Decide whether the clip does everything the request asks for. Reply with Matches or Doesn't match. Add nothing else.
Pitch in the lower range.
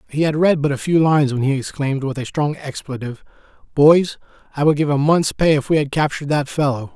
Doesn't match